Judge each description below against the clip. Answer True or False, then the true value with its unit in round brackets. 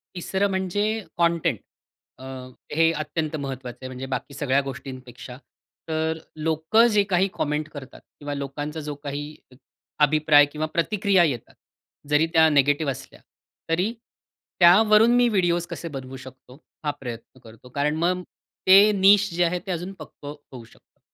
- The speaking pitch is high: False (155 Hz)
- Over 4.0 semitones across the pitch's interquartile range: True (4.7 semitones)